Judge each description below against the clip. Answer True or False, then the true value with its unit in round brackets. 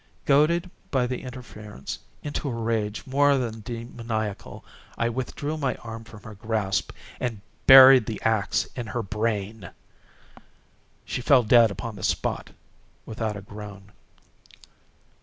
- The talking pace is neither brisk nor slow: False (130 wpm)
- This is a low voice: True (115 Hz)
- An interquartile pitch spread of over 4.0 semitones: False (3.2 semitones)